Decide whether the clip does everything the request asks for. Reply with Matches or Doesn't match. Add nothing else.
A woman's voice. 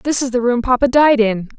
Matches